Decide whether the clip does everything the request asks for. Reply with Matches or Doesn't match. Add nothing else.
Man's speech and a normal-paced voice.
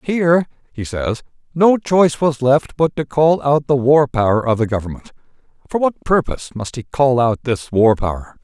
Matches